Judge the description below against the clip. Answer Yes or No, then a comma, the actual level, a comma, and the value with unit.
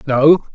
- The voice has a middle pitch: Yes, medium, 145 Hz